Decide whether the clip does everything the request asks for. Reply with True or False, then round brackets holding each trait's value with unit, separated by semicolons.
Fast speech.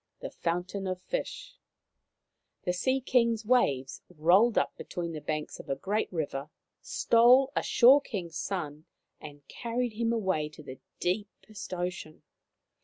False (135 wpm)